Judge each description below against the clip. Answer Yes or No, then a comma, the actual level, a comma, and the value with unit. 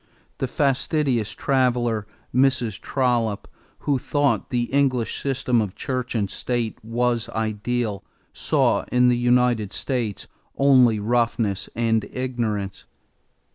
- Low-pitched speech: Yes, low, 120 Hz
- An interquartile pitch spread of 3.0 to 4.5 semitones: No, narrow, 2.4 semitones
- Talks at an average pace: No, slow, 110 wpm